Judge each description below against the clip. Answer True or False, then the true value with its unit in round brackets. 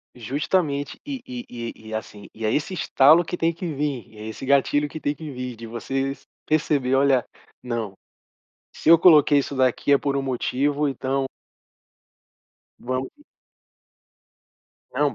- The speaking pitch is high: False (135 Hz)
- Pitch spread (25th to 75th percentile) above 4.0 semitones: False (3.0 semitones)